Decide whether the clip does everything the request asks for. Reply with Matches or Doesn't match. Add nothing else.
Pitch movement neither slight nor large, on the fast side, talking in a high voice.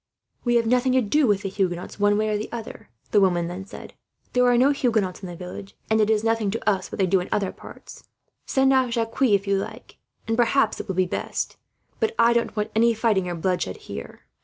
Matches